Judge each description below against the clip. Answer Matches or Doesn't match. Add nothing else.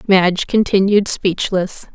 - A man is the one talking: Doesn't match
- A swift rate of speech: Doesn't match